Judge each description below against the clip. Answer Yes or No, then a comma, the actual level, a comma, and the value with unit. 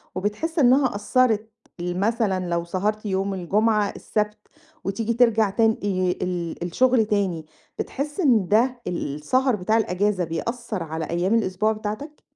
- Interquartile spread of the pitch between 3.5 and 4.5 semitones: Yes, average, 4.0 semitones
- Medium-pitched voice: No, high, 210 Hz